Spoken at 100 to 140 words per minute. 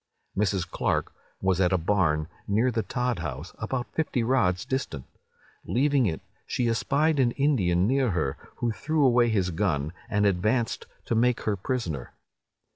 No: average, 155 wpm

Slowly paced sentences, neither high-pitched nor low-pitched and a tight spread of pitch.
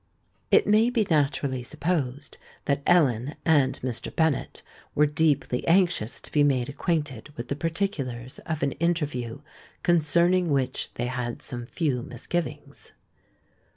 No: slow, 130 wpm; medium, 145 Hz; average, 4.9 semitones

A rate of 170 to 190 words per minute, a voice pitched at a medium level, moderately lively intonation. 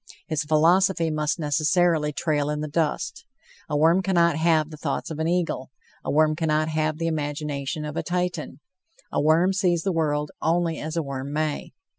No: average, 180 wpm; medium, 155 Hz; narrow, 2.0 semitones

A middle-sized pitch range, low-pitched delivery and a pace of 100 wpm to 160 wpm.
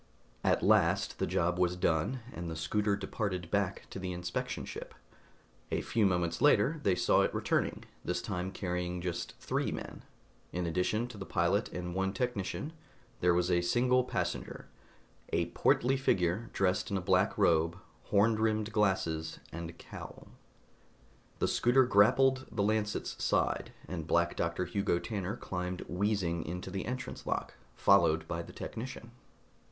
Yes: average, 3.6 semitones; very low, 95 Hz; average, 155 wpm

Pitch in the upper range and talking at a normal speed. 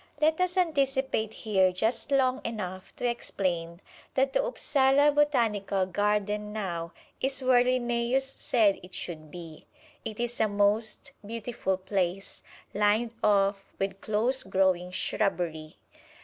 No: high, 210 Hz; slow, 125 wpm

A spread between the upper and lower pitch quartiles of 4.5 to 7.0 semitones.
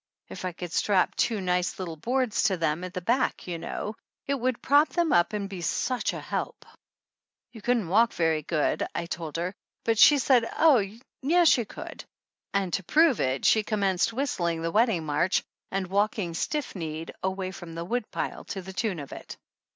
Yes: wide, 5.6 semitones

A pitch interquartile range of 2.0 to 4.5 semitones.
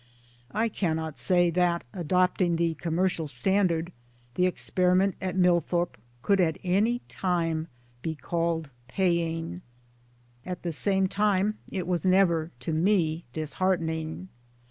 Yes: narrow, 2.4 semitones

